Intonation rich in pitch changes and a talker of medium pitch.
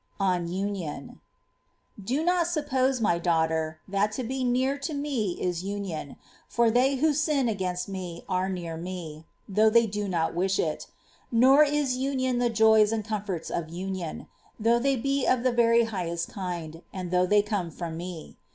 No: wide, 6.1 semitones; high, 205 Hz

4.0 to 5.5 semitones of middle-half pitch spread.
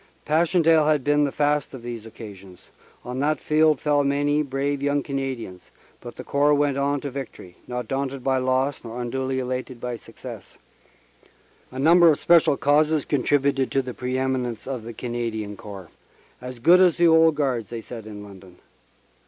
No: average, 3.3 semitones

